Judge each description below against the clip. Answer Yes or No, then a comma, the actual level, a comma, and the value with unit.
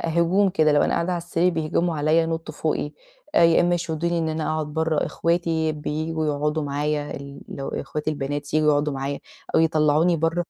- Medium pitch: Yes, medium, 155 Hz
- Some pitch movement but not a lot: No, narrow, 2.0 semitones